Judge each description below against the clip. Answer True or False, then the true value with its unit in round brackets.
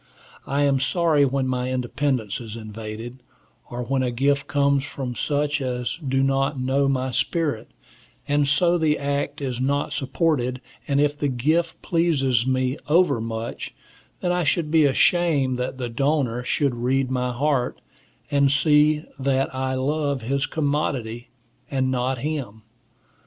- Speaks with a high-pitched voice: False (135 Hz)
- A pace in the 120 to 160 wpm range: True (145 wpm)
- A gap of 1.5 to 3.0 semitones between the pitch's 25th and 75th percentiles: True (2.7 semitones)